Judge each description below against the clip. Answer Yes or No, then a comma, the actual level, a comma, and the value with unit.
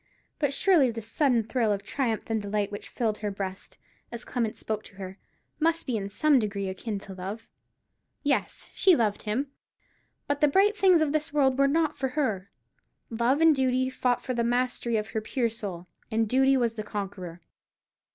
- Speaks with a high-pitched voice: Yes, high, 235 Hz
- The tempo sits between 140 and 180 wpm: No, average, 190 wpm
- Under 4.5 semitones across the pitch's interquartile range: No, average, 4.8 semitones